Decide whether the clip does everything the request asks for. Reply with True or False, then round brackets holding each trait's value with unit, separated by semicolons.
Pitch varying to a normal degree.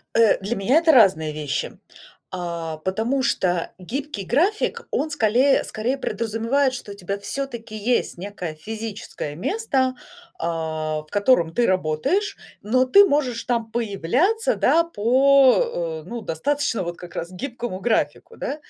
False (7.0 semitones)